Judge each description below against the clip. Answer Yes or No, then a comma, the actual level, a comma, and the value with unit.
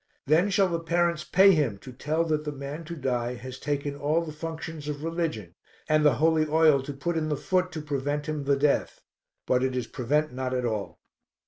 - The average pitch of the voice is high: No, medium, 150 Hz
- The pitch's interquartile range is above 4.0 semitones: No, average, 3.4 semitones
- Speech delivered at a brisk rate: Yes, fast, 215 wpm